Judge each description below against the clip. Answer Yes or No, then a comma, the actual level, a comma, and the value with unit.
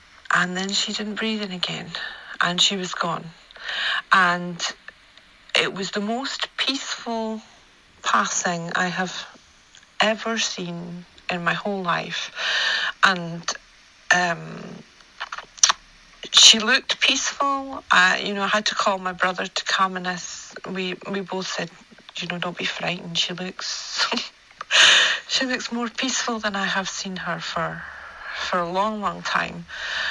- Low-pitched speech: No, high, 195 Hz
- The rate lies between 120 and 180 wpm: Yes, average, 140 wpm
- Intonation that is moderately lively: Yes, average, 3.4 semitones